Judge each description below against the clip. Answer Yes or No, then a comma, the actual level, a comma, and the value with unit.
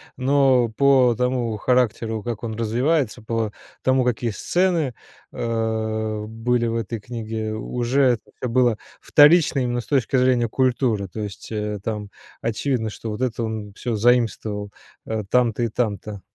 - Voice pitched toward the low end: Yes, low, 115 Hz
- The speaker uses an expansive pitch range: No, narrow, 2.5 semitones